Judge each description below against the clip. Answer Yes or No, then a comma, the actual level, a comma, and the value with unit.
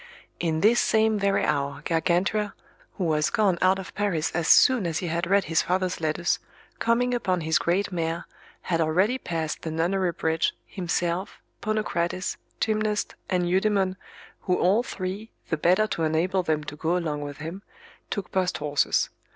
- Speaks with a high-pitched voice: No, medium, 180 Hz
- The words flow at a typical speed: Yes, average, 165 wpm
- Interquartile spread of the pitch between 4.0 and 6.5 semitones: No, average, 3.5 semitones